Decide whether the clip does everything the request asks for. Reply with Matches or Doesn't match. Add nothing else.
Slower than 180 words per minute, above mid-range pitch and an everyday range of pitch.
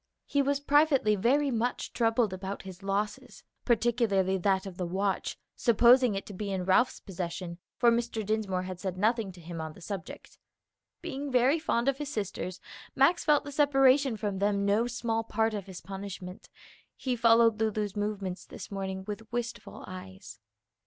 Matches